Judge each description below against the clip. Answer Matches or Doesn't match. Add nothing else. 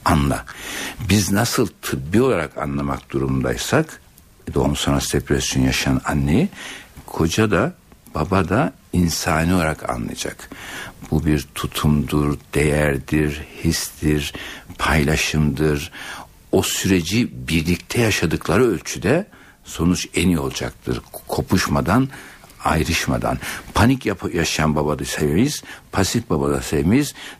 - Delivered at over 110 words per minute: Doesn't match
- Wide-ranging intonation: Doesn't match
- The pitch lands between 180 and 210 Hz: Doesn't match